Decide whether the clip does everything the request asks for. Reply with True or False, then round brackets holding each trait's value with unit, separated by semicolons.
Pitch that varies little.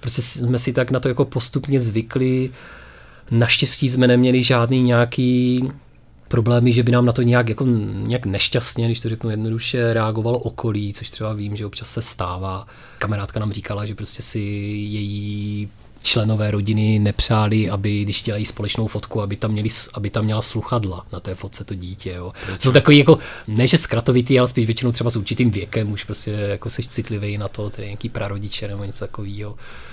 False (3.0 semitones)